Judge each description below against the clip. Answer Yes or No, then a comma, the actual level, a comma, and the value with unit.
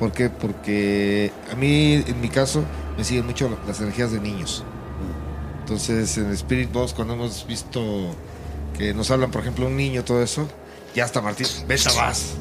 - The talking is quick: No, average, 170 wpm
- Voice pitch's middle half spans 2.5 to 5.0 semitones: Yes, average, 3.8 semitones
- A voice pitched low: Yes, low, 110 Hz